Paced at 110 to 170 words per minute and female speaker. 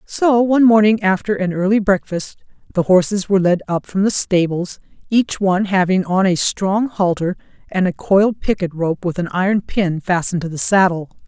No: average, 185 wpm; female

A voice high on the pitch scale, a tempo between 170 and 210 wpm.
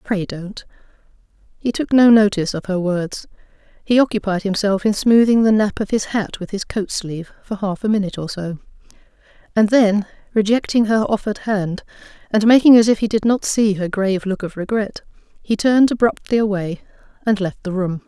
Yes: high, 205 Hz; average, 185 wpm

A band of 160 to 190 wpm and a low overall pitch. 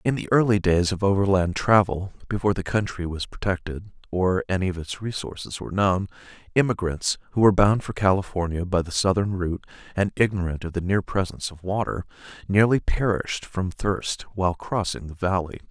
Yes: average, 170 wpm; very low, 95 Hz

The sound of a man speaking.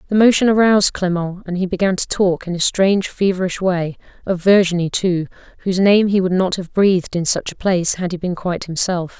No: female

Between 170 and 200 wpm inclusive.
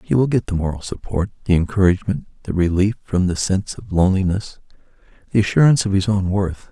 Yes: average, 190 wpm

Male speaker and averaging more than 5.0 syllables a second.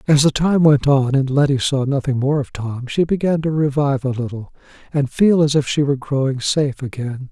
Yes: male; 5.5 syllables/s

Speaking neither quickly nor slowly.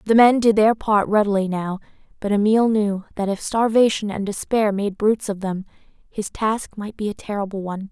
Yes: average, 195 wpm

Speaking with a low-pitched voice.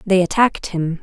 No: medium, 185 Hz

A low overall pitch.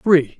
No: medium, 160 Hz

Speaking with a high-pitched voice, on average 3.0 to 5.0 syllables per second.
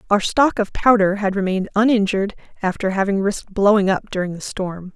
No: high, 200 Hz; 5.9 syllables/s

